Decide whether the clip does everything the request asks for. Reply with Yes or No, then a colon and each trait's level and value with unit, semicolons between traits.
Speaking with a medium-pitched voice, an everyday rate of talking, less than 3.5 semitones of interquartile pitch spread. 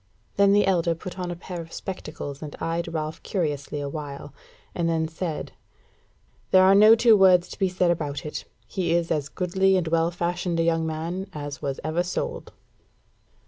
Yes: medium, 170 Hz; average, 185 wpm; average, 2.8 semitones